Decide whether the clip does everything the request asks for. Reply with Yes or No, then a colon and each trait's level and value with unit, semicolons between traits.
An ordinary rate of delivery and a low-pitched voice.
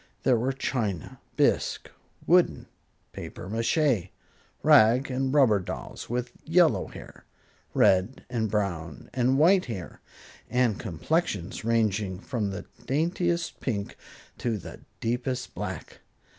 No: slow, 115 wpm; low, 120 Hz